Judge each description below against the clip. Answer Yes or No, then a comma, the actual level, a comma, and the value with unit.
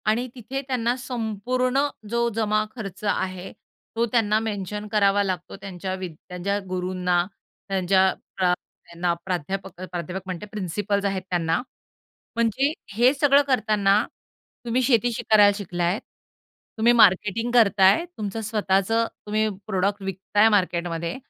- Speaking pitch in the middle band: No, high, 205 Hz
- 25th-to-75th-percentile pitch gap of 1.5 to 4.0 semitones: Yes, average, 3.4 semitones